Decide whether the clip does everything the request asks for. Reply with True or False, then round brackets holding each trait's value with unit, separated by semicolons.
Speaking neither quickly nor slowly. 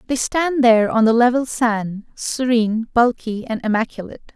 True (150 wpm)